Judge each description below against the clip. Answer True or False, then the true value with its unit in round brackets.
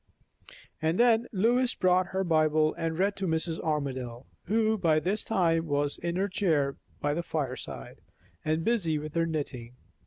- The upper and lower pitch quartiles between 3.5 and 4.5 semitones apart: True (3.8 semitones)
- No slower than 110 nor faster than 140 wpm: False (160 wpm)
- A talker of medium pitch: True (165 Hz)